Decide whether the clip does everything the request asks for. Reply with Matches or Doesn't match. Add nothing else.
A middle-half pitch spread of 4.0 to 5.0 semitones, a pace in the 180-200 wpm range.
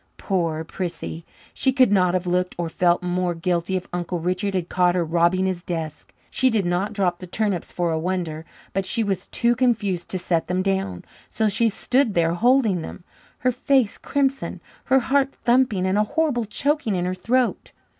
Matches